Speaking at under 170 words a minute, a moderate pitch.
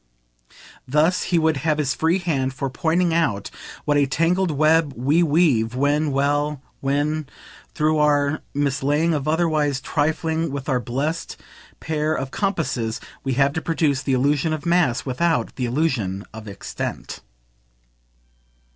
Yes: average, 140 wpm; medium, 150 Hz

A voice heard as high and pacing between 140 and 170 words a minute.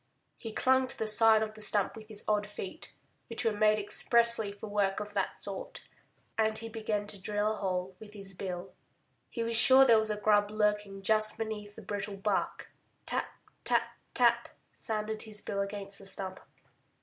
No: high, 210 Hz; average, 185 wpm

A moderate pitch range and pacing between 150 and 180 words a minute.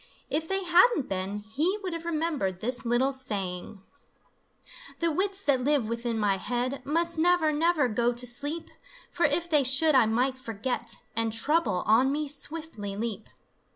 No: wide, 6.1 semitones; average, 160 wpm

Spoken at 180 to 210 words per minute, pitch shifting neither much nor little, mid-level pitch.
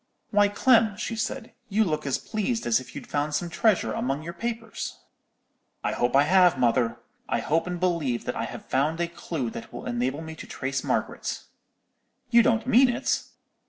No: average, 190 wpm; wide, 8.4 semitones; medium, 170 Hz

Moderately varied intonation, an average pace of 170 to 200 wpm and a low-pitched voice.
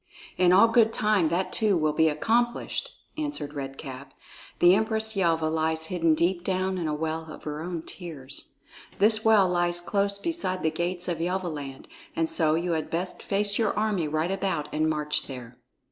No: average, 4.0 semitones; average, 180 wpm; medium, 175 Hz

